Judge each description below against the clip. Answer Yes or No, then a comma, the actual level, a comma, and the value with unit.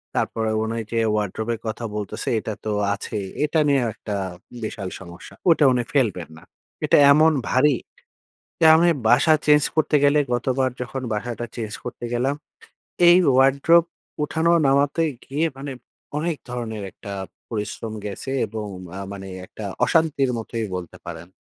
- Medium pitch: No, low, 120 Hz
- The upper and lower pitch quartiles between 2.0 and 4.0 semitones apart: No, average, 5.0 semitones